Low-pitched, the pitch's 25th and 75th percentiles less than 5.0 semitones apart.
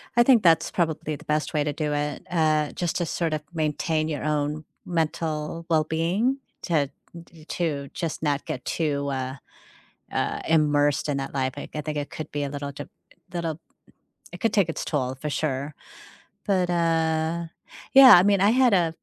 No: medium, 155 Hz; narrow, 2.4 semitones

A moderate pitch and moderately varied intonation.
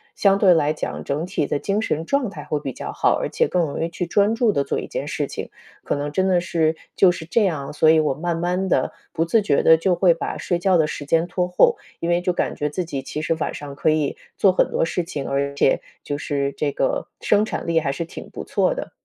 Yes: medium, 165 Hz; average, 3.7 semitones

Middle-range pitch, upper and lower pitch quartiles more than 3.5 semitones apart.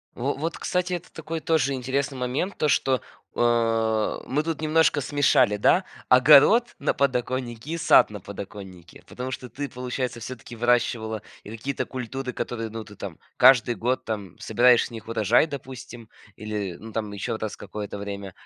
No: low, 120 Hz; average, 4.0 semitones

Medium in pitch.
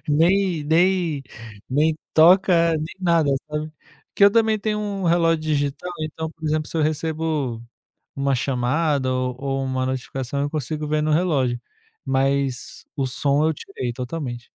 Yes: medium, 150 Hz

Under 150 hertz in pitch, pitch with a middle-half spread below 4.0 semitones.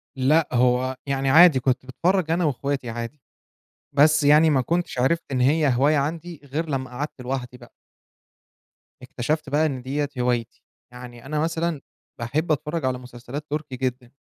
Yes: medium, 140 Hz; average, 3.4 semitones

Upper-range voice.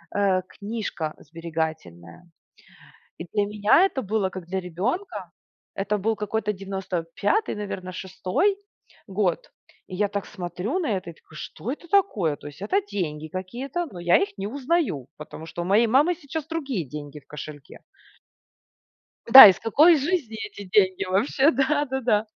Yes: high, 200 Hz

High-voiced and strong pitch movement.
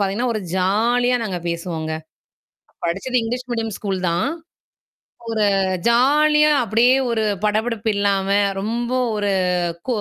No: high, 220 Hz; average, 3.8 semitones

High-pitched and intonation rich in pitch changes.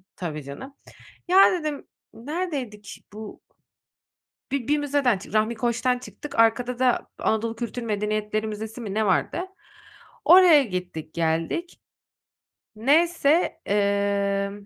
Yes: high, 225 Hz; wide, 5.7 semitones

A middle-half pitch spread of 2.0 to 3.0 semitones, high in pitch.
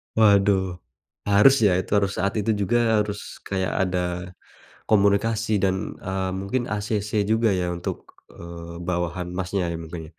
No: average, 2.7 semitones; very low, 95 Hz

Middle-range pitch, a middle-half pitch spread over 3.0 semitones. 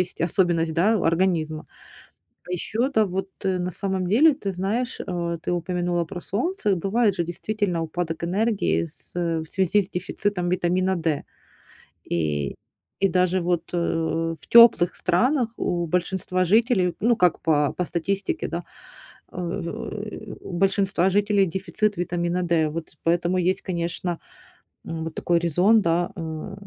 No: medium, 180 Hz; average, 2.7 semitones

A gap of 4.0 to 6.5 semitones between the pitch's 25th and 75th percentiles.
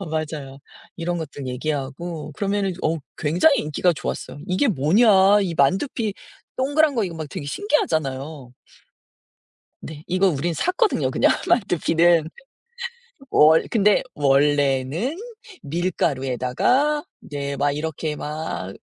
Yes: wide, 5.4 semitones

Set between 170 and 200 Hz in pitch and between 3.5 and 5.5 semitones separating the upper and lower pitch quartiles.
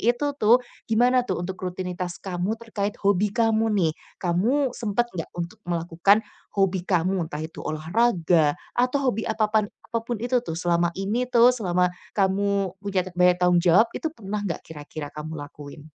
Yes: high, 190 Hz; average, 4.4 semitones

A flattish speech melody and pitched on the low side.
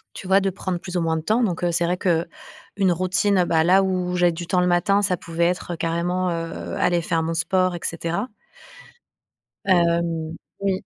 No: narrow, 1.8 semitones; medium, 175 Hz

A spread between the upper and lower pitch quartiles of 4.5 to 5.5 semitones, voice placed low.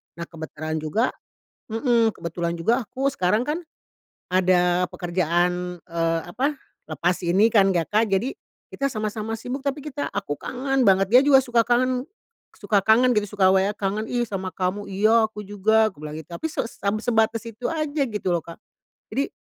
No: average, 5.2 semitones; high, 210 Hz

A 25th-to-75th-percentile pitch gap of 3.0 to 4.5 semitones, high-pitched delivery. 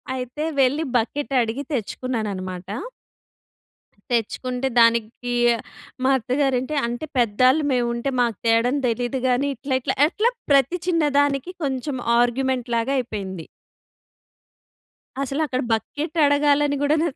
Yes: average, 3.4 semitones; very high, 255 Hz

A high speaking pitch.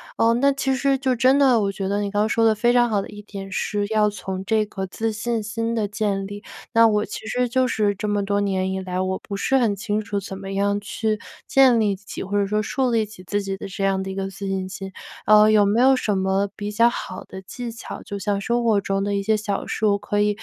Yes: high, 205 Hz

